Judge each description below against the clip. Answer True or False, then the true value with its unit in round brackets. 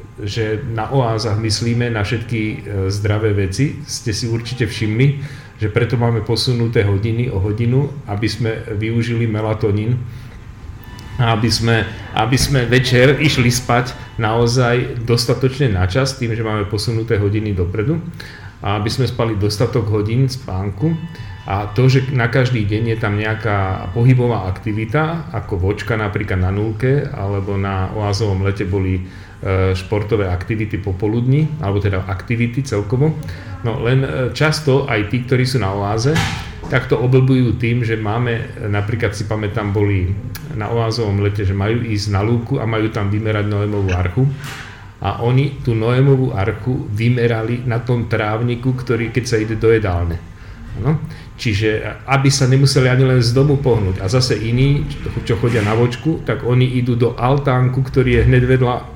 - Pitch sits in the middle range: False (115 Hz)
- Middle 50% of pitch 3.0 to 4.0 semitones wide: True (3.3 semitones)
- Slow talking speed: False (150 wpm)